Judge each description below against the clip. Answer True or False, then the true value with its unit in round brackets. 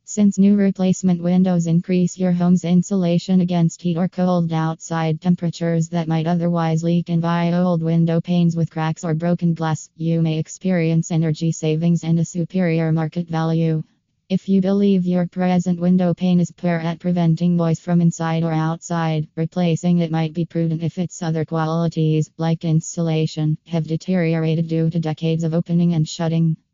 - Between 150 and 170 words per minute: True (165 wpm)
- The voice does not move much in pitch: True (1.5 semitones)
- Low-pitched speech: False (165 Hz)